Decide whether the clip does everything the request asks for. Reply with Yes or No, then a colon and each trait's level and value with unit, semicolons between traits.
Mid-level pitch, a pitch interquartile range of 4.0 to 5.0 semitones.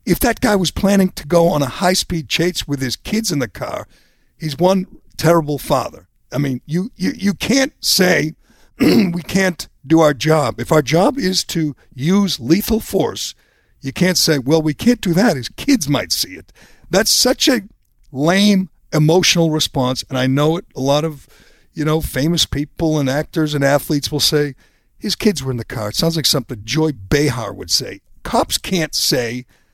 Yes: medium, 155 Hz; average, 4.4 semitones